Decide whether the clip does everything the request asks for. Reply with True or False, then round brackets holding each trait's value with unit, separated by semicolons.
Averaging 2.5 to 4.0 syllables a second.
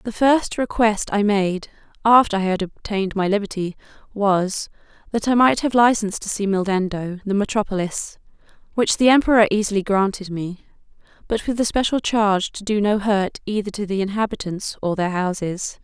False (5.2 syllables/s)